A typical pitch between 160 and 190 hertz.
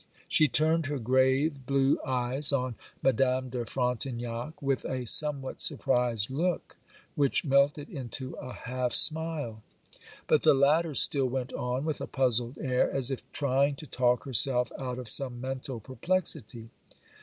No: low, 130 Hz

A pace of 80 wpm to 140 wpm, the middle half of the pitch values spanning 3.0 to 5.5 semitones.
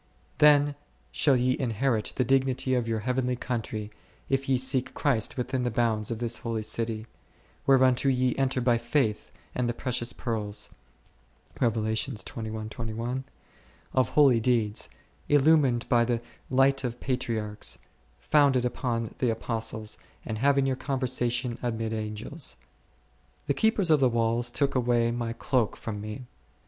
No: slow, 135 wpm; narrow, 2.6 semitones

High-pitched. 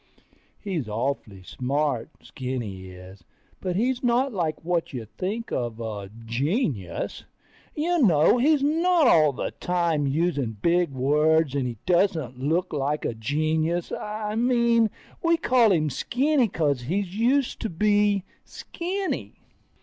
No: medium, 165 Hz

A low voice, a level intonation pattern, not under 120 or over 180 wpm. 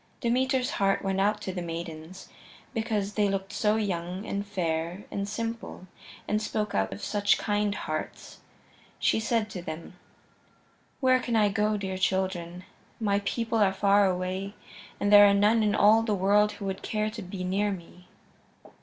No: high, 200 Hz; narrow, 2.2 semitones; average, 170 wpm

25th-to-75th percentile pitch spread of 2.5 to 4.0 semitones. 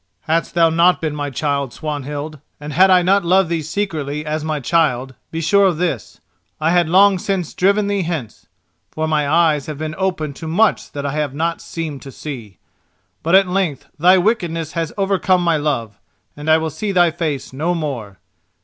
Yes: average, 3.4 semitones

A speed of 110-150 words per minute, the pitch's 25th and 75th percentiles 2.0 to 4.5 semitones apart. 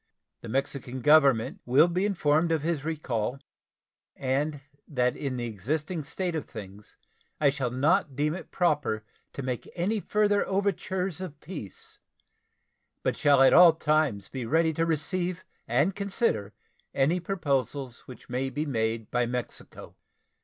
No: average, 145 wpm; average, 5.1 semitones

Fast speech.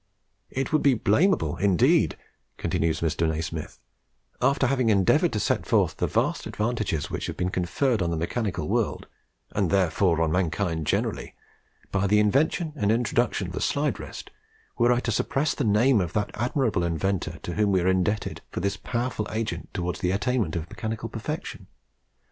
No: average, 170 wpm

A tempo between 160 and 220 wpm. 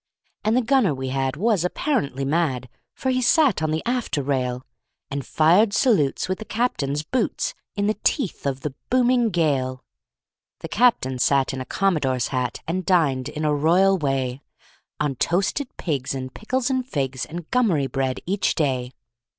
Yes: average, 165 wpm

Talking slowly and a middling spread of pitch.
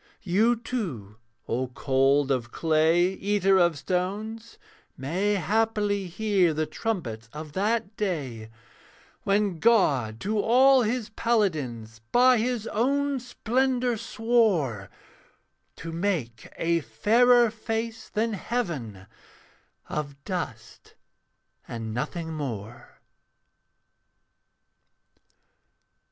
No: slow, 90 wpm; wide, 8.2 semitones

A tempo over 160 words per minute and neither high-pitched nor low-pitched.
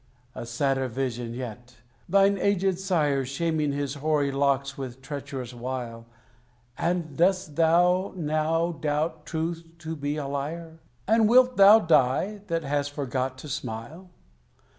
No: slow, 135 wpm; medium, 150 Hz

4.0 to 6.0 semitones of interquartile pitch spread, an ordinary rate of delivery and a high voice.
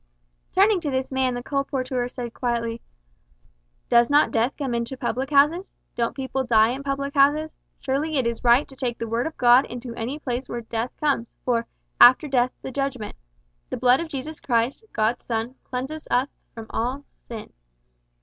No: average, 2.8 semitones; average, 180 wpm; very high, 255 Hz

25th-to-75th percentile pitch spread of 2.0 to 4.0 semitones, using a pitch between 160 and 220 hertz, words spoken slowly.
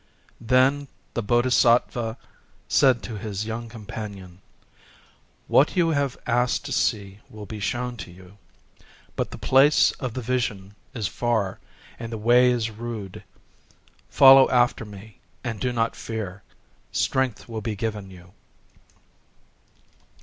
No: average, 3.2 semitones; low, 115 Hz; slow, 130 wpm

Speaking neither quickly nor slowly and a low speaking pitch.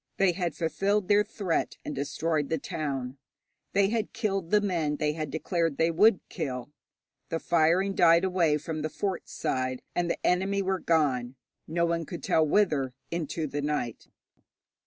No: average, 165 wpm; medium, 165 Hz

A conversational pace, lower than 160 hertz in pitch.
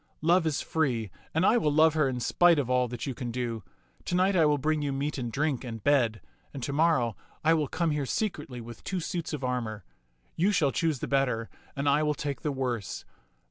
No: fast, 230 wpm; medium, 140 Hz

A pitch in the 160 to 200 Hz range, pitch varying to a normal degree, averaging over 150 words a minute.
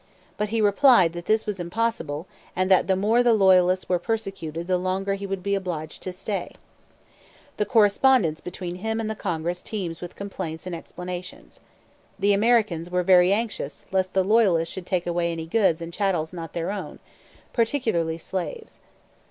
Yes: medium, 185 Hz; average, 3.3 semitones; average, 170 wpm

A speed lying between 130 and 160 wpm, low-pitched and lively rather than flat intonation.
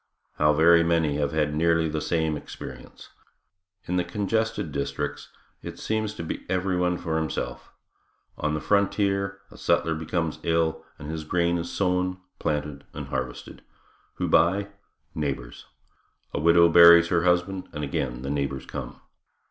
No: average, 150 wpm; very low, 85 Hz; average, 3.0 semitones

